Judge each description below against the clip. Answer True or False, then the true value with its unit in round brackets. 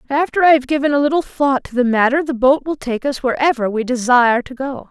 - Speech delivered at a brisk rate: True (245 wpm)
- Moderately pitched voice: False (265 Hz)